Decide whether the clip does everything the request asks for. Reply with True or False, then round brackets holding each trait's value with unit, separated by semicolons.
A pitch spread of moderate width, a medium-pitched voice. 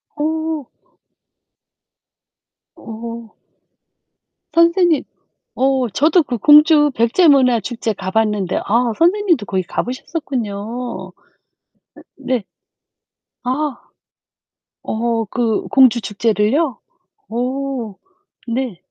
False (4.9 semitones; 245 Hz)